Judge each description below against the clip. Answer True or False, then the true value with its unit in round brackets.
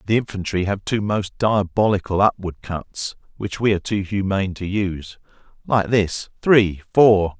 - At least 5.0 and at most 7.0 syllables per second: False (4.6 syllables/s)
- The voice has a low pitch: True (100 Hz)